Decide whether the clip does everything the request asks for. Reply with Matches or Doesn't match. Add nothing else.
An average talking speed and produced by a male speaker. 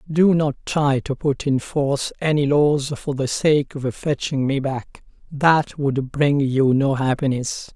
Matches